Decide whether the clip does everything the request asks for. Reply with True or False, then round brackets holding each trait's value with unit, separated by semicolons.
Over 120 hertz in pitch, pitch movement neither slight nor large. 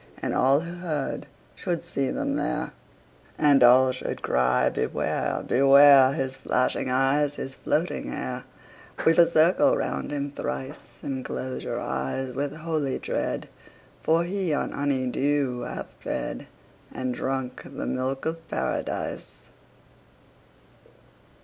True (135 Hz; 3.3 semitones)